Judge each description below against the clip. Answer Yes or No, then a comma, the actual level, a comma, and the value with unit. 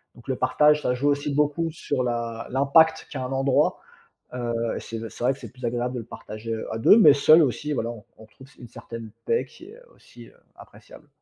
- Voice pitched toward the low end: Yes, low, 130 Hz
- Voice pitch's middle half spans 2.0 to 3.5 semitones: No, average, 3.9 semitones